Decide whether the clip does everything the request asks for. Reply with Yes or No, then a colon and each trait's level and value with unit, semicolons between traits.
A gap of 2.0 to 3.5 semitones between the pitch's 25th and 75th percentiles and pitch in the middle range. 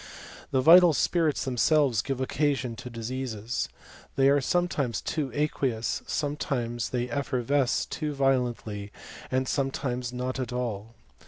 No: average, 3.0 semitones; low, 130 Hz